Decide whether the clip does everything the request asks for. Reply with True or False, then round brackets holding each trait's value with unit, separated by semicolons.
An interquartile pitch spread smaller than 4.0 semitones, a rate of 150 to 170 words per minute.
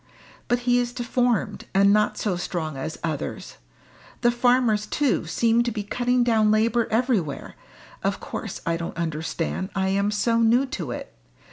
False (4.5 semitones; 160 wpm)